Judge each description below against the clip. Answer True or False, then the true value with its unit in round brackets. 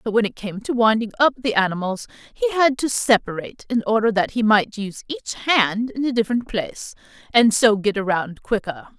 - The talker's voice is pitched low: False (220 Hz)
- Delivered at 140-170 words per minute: False (200 wpm)